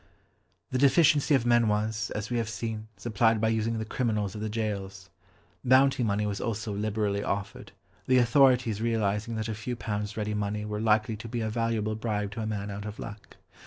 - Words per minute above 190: Yes, average, 200 wpm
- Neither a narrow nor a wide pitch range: No, narrow, 1.8 semitones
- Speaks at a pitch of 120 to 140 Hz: No, low, 110 Hz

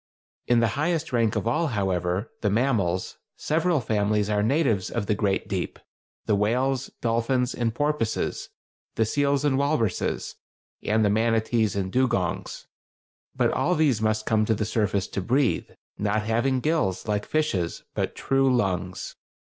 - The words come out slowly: No, average, 150 wpm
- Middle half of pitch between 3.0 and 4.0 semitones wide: No, average, 4.5 semitones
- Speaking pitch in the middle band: No, low, 115 Hz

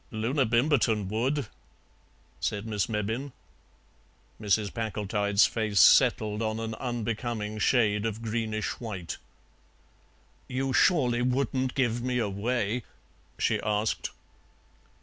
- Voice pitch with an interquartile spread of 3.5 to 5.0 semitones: No, average, 2.8 semitones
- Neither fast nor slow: No, slow, 100 wpm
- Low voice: Yes, low, 115 Hz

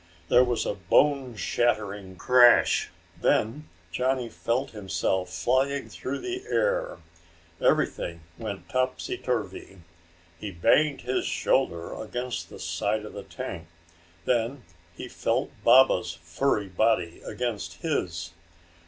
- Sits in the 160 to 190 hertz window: No, low, 120 Hz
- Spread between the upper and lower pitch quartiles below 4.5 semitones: No, average, 5.2 semitones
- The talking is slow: Yes, slow, 115 wpm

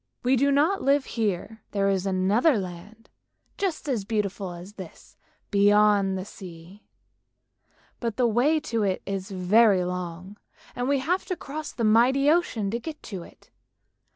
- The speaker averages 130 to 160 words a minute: Yes, average, 155 wpm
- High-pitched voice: Yes, high, 210 Hz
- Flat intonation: No, wide, 5.5 semitones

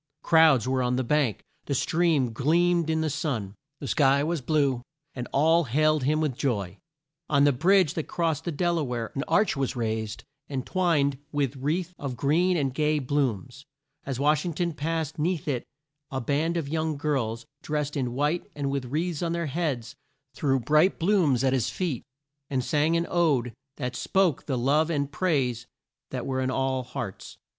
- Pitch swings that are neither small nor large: Yes, average, 3.7 semitones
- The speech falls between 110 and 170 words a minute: No, average, 185 wpm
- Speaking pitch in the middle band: Yes, medium, 145 Hz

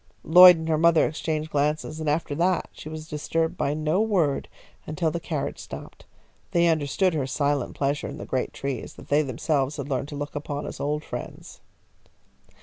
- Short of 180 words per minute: No, average, 185 wpm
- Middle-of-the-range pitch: Yes, medium, 155 Hz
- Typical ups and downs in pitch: No, narrow, 2.1 semitones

